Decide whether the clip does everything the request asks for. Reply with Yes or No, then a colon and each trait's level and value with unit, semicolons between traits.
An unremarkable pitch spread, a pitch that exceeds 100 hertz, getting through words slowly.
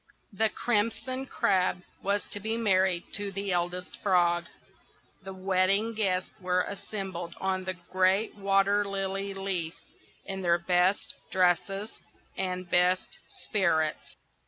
No: narrow, 1.7 semitones; high, 190 Hz; slow, 120 wpm